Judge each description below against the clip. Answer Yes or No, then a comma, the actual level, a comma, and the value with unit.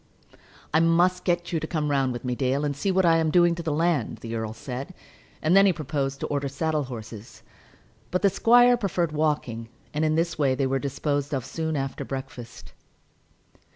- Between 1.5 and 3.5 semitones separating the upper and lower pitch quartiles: No, average, 4.1 semitones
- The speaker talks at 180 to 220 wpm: Yes, average, 200 wpm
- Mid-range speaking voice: Yes, medium, 150 Hz